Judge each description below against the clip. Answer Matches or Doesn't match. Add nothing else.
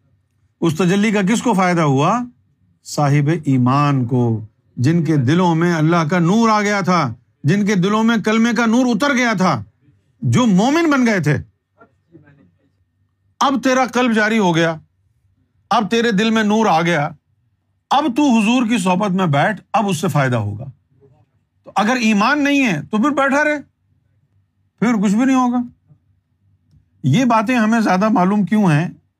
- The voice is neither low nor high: Matches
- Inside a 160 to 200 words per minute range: Matches